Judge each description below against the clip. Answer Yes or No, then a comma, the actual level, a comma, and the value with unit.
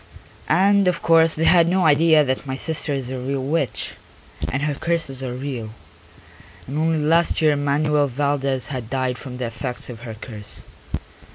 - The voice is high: No, medium, 140 Hz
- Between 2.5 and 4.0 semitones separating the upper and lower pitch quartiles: Yes, average, 3.7 semitones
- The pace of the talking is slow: No, average, 175 wpm